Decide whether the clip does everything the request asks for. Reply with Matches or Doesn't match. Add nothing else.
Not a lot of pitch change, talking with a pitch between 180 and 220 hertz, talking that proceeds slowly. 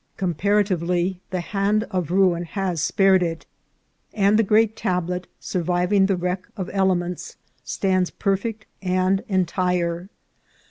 Matches